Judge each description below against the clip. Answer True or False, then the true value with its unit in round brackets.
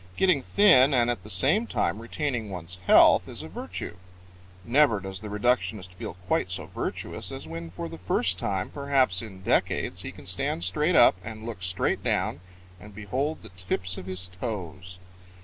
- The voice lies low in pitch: True (100 Hz)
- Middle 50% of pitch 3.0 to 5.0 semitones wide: False (5.4 semitones)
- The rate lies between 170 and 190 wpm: True (180 wpm)